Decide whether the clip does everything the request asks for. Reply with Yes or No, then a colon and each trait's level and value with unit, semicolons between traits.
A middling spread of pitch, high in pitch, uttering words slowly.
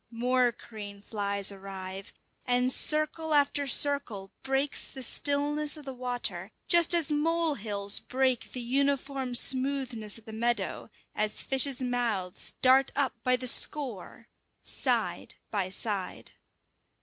Yes: average, 4.7 semitones; very high, 250 Hz; slow, 125 wpm